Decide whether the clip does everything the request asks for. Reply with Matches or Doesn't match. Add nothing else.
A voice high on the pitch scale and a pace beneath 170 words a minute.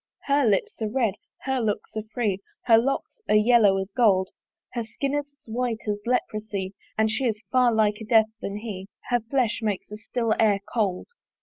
Doesn't match